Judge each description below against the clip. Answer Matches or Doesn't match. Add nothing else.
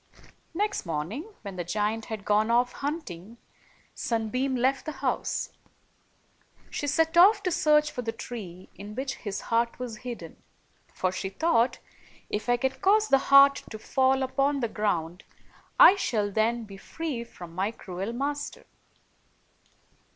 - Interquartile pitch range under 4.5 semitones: Doesn't match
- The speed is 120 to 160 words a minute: Matches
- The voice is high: Matches